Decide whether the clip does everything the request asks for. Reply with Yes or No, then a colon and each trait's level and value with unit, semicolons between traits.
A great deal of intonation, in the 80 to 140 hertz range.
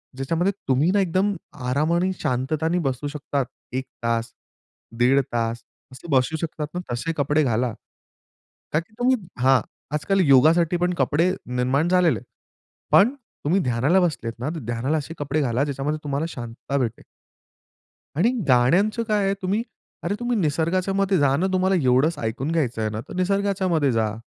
No: wide, 6.0 semitones; medium, 150 Hz